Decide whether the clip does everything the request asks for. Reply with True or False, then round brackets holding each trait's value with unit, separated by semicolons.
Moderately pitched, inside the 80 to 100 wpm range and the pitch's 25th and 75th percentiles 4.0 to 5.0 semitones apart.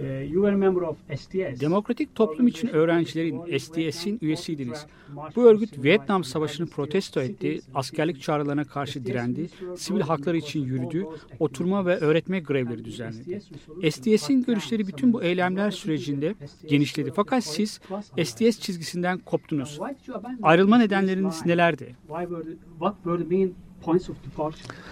True (170 Hz; 95 wpm; 4.4 semitones)